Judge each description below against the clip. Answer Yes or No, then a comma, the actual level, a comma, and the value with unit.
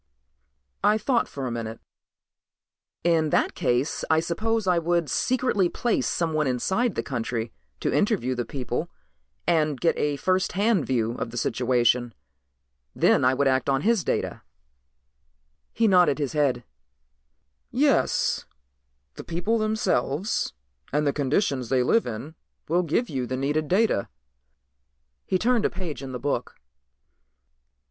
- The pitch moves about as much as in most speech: No, wide, 6.6 semitones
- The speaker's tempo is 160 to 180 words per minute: No, average, 140 wpm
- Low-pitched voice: No, medium, 150 Hz